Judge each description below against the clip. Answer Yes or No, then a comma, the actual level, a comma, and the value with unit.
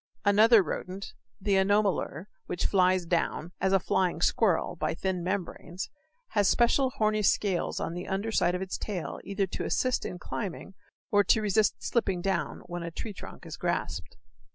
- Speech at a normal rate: Yes, average, 170 wpm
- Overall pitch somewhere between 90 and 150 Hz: No, high, 190 Hz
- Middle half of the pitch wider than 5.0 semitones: No, average, 2.7 semitones